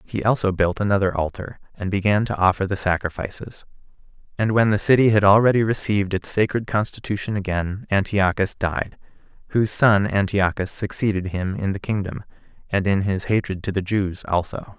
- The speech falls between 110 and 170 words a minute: Yes, average, 160 wpm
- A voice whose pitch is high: No, low, 100 Hz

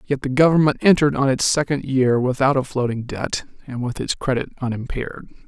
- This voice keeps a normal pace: Yes, average, 185 wpm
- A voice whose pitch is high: No, low, 135 Hz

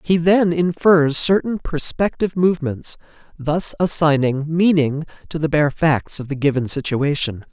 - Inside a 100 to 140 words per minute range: Yes, slow, 135 wpm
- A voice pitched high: No, medium, 155 Hz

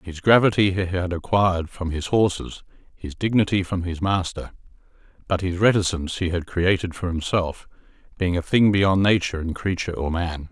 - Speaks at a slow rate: No, average, 170 wpm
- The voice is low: Yes, very low, 90 Hz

